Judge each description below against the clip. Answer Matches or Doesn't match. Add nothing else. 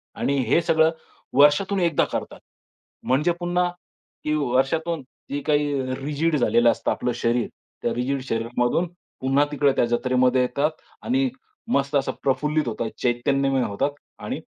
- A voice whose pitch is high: Doesn't match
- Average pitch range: Matches